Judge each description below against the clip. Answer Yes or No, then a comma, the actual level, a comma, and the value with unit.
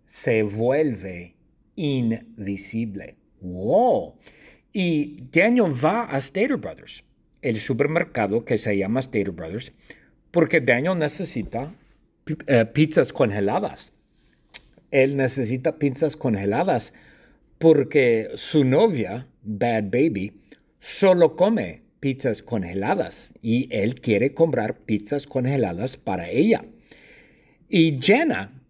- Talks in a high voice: No, low, 135 Hz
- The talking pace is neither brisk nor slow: No, slow, 100 wpm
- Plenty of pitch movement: Yes, wide, 6.0 semitones